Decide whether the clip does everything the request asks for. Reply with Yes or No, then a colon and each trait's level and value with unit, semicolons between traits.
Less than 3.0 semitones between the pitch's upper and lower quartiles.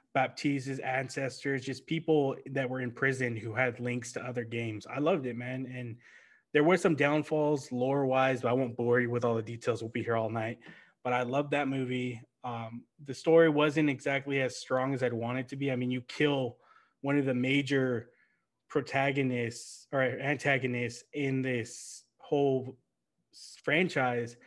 Yes: narrow, 2.4 semitones